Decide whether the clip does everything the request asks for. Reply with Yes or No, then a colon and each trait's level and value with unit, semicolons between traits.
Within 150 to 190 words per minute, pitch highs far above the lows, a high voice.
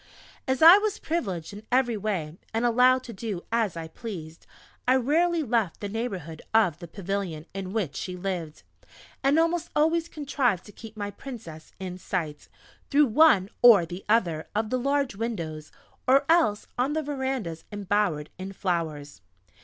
Yes: average, 160 wpm; wide, 6.9 semitones; high, 210 Hz